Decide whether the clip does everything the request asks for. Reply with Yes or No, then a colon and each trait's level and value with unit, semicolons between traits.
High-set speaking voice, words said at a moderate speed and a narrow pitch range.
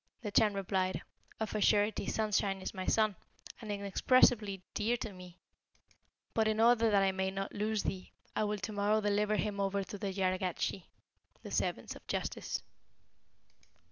Yes: high, 205 Hz; average, 165 wpm; narrow, 1.9 semitones